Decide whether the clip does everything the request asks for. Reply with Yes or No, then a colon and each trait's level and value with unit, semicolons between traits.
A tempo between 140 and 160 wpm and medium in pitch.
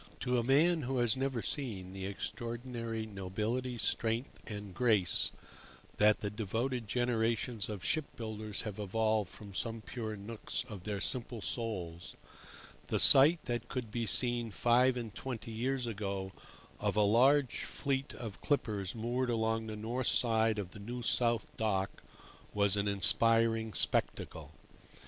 No: average, 145 wpm; low, 115 Hz